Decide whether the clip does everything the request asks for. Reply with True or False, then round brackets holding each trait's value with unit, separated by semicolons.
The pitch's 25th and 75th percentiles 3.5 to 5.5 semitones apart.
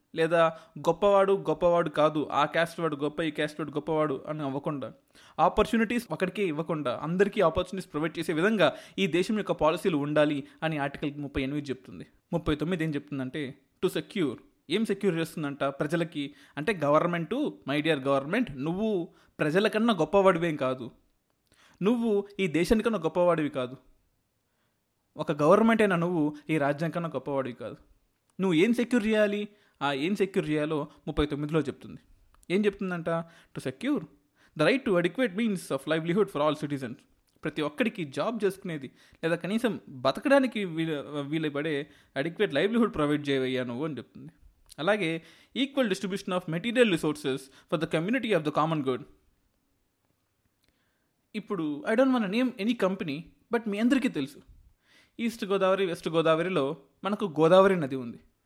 True (5.2 semitones)